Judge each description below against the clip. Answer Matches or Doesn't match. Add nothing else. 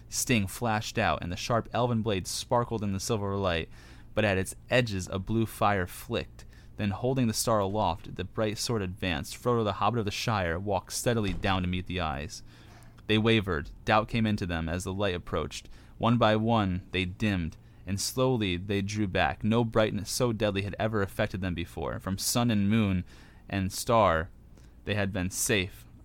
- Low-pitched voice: Matches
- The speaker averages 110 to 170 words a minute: Doesn't match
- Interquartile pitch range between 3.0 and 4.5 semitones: Matches